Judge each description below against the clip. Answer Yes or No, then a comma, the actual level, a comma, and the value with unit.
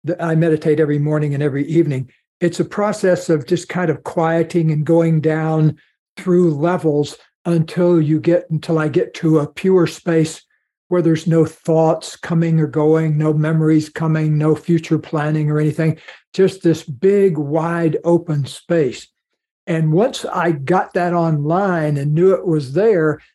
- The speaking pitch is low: No, medium, 160 Hz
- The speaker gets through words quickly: No, average, 160 wpm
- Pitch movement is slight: Yes, narrow, 1.8 semitones